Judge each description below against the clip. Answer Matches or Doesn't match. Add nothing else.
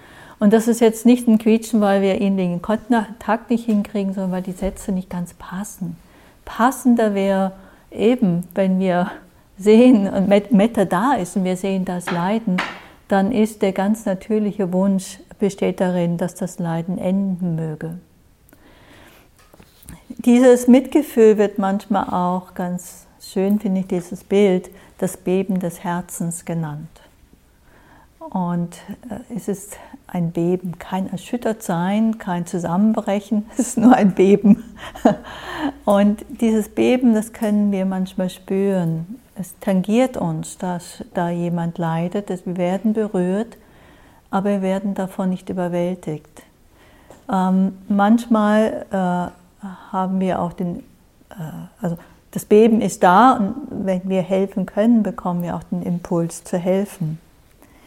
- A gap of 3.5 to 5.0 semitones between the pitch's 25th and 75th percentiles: Doesn't match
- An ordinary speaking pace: Doesn't match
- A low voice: Doesn't match